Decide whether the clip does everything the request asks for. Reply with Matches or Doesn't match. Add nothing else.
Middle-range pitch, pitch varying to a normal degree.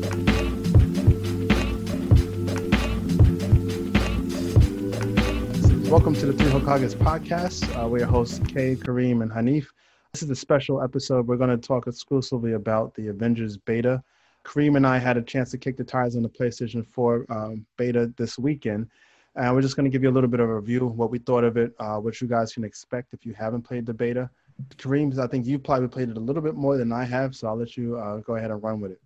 Doesn't match